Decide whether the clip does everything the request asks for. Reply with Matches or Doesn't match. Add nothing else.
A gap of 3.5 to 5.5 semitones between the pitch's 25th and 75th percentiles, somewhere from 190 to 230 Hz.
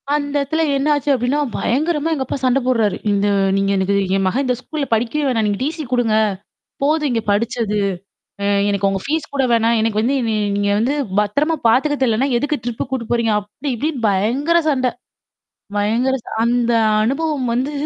Doesn't match